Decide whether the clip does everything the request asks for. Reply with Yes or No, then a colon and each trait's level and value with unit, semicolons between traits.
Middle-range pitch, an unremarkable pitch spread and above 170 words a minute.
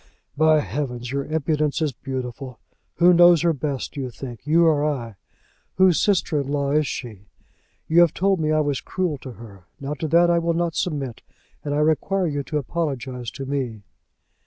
Yes: medium, 150 Hz; average, 3.8 semitones; average, 190 wpm